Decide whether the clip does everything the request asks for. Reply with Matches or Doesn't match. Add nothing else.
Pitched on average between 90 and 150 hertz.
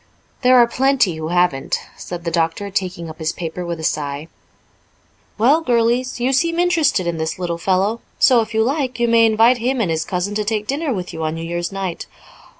Doesn't match